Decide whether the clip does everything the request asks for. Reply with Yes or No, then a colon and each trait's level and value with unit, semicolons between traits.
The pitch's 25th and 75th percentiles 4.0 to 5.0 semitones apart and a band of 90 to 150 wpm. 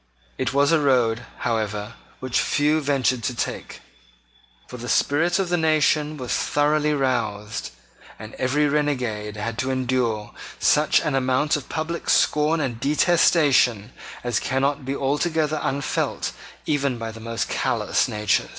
Yes: average, 4.3 semitones; average, 140 wpm